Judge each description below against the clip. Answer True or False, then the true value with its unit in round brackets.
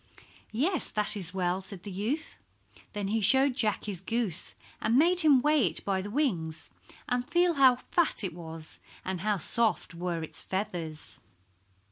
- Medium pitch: False (210 Hz)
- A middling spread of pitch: False (6.6 semitones)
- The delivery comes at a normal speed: True (165 wpm)